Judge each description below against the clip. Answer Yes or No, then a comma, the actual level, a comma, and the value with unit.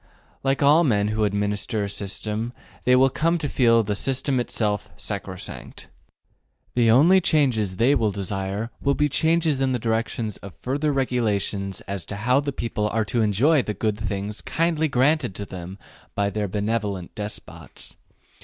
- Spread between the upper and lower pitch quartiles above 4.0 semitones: Yes, average, 4.8 semitones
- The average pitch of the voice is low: Yes, low, 115 Hz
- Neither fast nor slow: Yes, average, 165 wpm